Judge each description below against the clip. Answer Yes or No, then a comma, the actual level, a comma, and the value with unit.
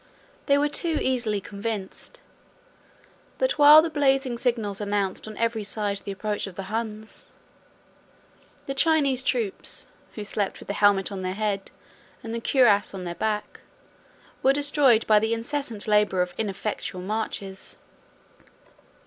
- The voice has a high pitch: Yes, high, 215 Hz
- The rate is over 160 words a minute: No, average, 140 wpm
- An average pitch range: Yes, average, 4.6 semitones